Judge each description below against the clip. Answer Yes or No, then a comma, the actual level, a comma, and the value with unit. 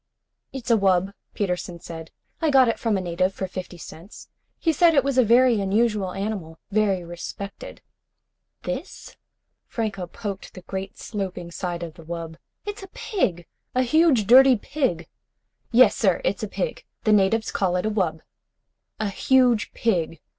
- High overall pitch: Yes, high, 200 Hz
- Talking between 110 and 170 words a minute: Yes, average, 160 wpm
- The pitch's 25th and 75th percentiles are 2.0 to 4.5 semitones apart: No, average, 5.2 semitones